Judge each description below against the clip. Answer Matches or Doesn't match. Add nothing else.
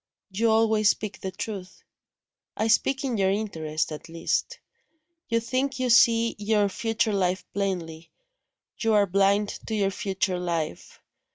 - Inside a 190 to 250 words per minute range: Doesn't match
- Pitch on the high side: Matches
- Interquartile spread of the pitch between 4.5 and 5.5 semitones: Doesn't match